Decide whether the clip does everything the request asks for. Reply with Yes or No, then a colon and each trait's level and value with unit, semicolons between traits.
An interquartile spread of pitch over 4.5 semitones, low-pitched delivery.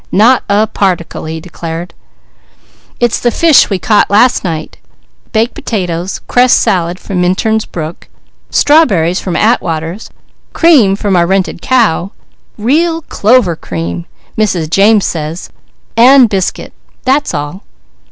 No: wide, 5.5 semitones; high, 195 Hz